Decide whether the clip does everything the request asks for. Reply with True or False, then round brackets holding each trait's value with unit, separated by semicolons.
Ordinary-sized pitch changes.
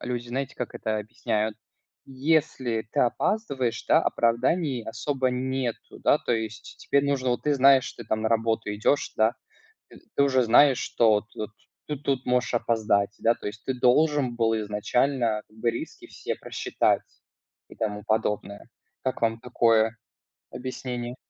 True (3.0 semitones)